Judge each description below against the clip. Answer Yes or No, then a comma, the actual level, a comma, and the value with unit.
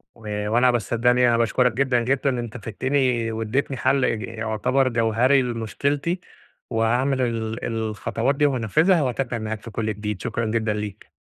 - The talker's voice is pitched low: Yes, low, 120 Hz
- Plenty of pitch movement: No, average, 2.8 semitones